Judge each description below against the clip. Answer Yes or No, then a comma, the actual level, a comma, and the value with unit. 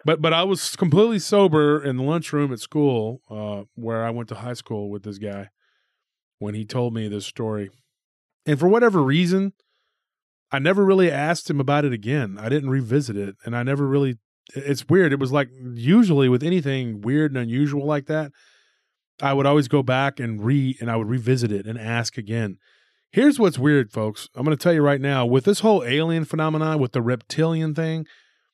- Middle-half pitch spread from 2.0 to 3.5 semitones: No, average, 5.0 semitones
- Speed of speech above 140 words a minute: Yes, average, 200 wpm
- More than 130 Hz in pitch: Yes, medium, 140 Hz